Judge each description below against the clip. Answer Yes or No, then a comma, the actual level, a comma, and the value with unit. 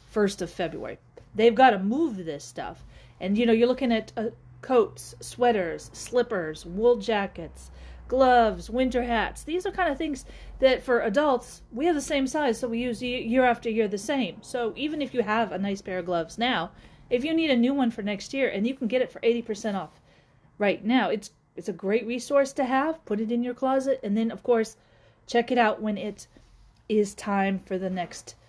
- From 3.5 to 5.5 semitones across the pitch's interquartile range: Yes, average, 4.4 semitones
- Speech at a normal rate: No, fast, 215 wpm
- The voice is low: No, high, 230 Hz